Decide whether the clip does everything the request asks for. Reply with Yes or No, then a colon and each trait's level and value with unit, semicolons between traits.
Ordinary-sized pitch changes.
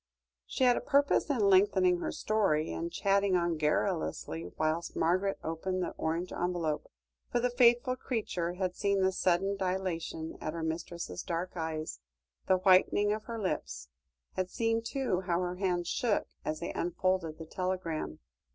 Yes: average, 3.4 semitones